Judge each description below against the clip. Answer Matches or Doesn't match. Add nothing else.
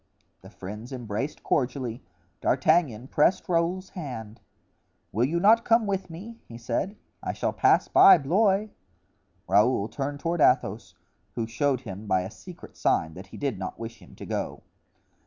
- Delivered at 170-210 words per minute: Doesn't match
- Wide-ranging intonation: Matches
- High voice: Doesn't match